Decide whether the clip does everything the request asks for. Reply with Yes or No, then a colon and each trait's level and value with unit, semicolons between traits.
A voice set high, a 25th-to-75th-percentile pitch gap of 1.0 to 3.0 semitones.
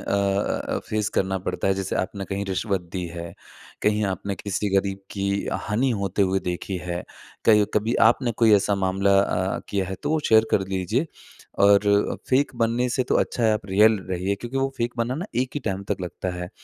No: low, 100 Hz; narrow, 2.6 semitones